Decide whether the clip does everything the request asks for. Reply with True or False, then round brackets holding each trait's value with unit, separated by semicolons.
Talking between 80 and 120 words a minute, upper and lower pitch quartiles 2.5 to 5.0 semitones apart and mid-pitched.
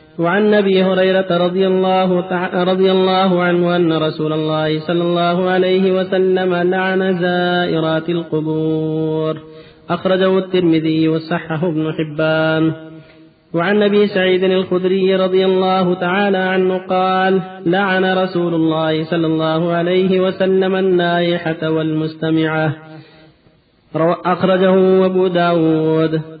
True (100 wpm; 2.8 semitones; 175 Hz)